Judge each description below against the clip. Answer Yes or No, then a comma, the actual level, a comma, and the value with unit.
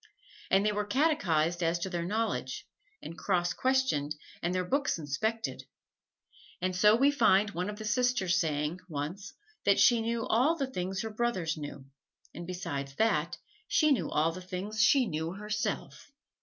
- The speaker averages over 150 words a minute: Yes, average, 165 wpm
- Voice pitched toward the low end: No, high, 190 Hz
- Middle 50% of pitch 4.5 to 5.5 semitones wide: Yes, average, 5.0 semitones